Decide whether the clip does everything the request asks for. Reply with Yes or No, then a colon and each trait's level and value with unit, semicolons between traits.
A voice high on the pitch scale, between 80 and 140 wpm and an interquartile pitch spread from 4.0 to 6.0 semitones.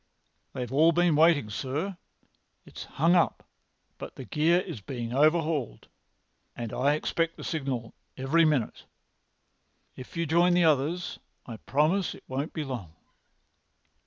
No: medium, 150 Hz; slow, 135 wpm; average, 4.3 semitones